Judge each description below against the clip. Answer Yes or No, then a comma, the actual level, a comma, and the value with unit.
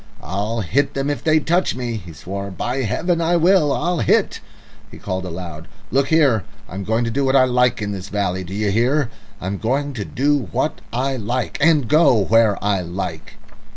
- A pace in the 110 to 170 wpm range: No, average, 195 wpm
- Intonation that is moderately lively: No, wide, 6.1 semitones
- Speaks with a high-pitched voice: No, low, 115 Hz